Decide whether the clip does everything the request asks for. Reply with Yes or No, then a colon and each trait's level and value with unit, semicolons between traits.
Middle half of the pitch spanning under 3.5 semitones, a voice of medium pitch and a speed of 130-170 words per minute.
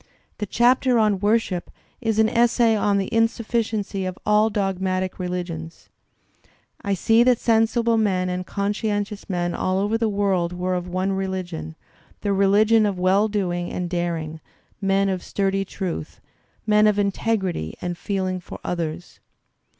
No: average, 2.9 semitones; high, 195 Hz; average, 150 wpm